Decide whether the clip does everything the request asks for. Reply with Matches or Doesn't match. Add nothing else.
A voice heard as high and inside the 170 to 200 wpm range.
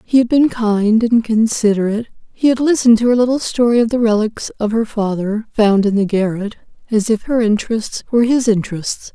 Matches